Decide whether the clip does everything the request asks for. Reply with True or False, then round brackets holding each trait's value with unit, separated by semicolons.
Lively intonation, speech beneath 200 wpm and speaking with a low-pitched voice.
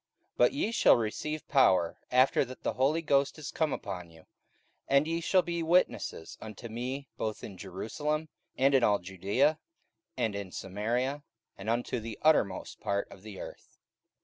True (6.8 semitones; 170 wpm; 125 Hz)